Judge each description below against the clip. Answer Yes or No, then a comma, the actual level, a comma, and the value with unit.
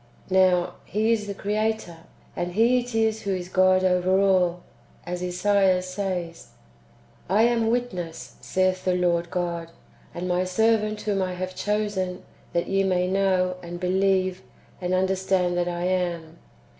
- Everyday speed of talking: Yes, average, 155 wpm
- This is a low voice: No, medium, 185 Hz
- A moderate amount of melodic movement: No, narrow, 2.1 semitones